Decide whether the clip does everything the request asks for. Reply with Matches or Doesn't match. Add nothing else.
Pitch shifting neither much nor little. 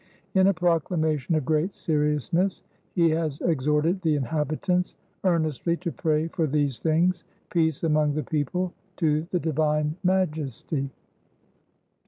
Doesn't match